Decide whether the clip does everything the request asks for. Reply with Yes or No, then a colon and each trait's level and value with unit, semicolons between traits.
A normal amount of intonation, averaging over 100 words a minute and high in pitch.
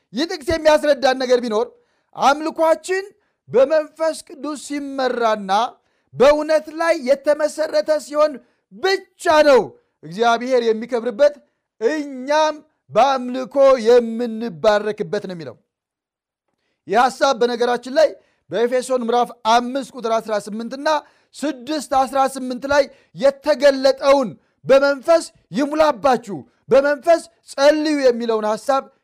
No: average, 4.0 semitones; average, 85 wpm; very high, 275 Hz